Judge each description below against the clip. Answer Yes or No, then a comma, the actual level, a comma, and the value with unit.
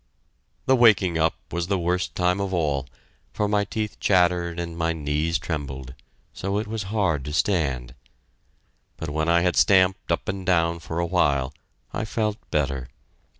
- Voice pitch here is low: Yes, very low, 85 Hz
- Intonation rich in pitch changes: No, average, 3.7 semitones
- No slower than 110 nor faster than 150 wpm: No, average, 165 wpm